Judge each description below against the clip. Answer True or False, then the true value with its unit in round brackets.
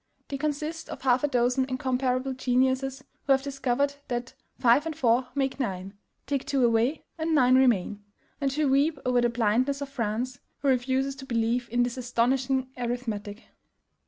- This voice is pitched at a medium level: False (255 Hz)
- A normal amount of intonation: False (2.1 semitones)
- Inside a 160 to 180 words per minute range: True (165 wpm)